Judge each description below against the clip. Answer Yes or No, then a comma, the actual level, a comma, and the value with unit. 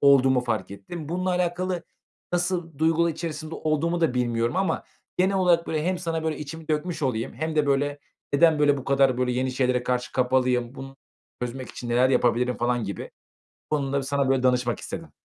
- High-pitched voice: No, medium, 140 Hz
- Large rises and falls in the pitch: No, average, 4.6 semitones